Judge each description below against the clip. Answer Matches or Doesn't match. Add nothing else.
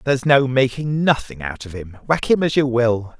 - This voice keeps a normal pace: Doesn't match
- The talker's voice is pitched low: Matches